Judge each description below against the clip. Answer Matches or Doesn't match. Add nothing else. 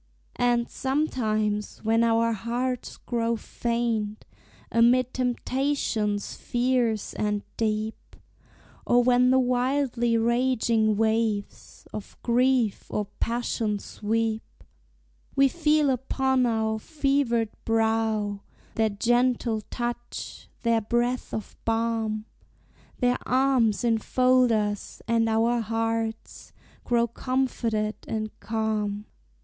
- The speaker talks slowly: Matches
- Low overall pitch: Doesn't match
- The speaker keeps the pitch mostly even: Matches